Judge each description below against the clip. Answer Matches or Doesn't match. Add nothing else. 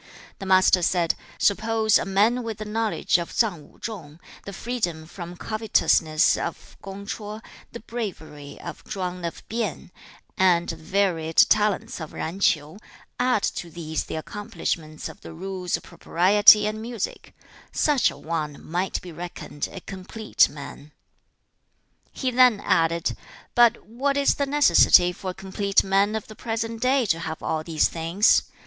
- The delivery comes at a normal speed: Matches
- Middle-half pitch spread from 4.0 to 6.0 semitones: Matches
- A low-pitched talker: Doesn't match